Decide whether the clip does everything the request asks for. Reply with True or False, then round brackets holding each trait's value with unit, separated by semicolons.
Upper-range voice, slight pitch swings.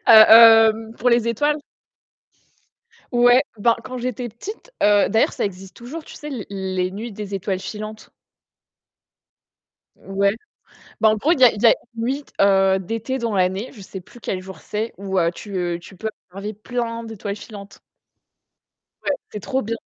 False (215 Hz; 3.3 semitones)